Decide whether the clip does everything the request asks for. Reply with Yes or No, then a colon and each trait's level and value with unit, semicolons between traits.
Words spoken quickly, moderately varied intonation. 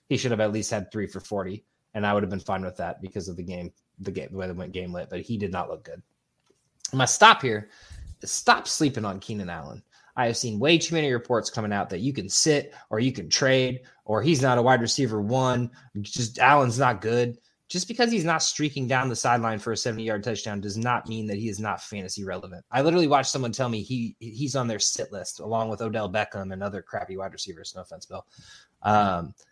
Yes: fast, 240 wpm; average, 4.4 semitones